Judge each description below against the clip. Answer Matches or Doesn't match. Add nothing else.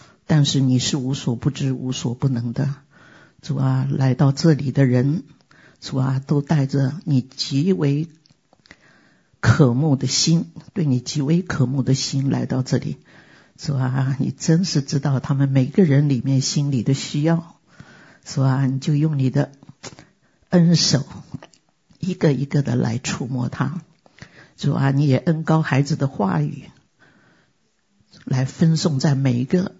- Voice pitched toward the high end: Doesn't match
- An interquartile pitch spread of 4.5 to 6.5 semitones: Doesn't match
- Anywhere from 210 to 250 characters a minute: Doesn't match